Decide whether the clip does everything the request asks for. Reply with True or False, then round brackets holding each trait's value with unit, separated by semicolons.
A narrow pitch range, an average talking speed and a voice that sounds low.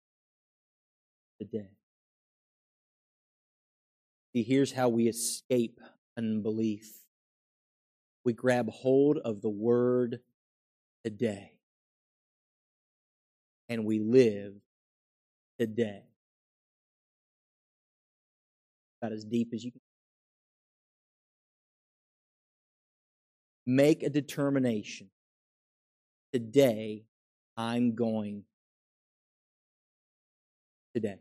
False (2.3 semitones; 60 wpm; 115 Hz)